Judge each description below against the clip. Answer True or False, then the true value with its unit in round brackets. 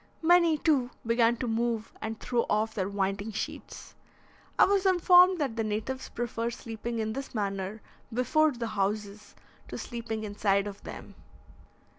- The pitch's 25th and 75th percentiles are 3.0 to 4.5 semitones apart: True (3.5 semitones)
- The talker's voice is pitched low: False (230 Hz)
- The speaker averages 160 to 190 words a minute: False (150 wpm)